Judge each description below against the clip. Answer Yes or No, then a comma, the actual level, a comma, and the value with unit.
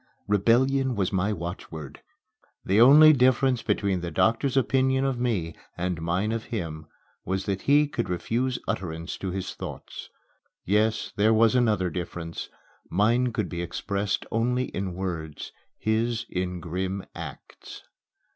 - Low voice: Yes, low, 105 Hz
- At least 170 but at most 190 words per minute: No, slow, 135 wpm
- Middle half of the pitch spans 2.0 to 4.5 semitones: No, average, 5.2 semitones